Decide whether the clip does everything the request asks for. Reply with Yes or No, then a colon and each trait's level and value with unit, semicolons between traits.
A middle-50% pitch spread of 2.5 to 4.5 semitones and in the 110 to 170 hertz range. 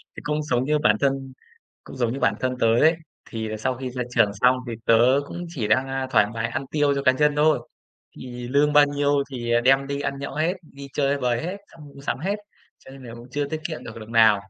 Yes: average, 3.4 semitones; low, 135 Hz